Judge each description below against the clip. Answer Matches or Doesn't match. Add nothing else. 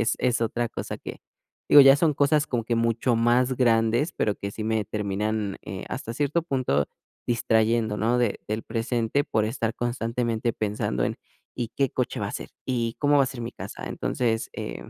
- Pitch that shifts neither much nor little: Doesn't match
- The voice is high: Doesn't match